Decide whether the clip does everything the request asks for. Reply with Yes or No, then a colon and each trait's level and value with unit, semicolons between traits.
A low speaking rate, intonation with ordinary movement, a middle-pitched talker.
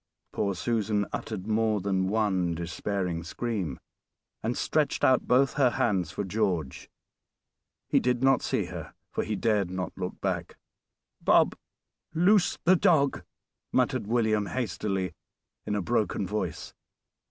No: slow, 130 wpm; average, 4.4 semitones; low, 105 Hz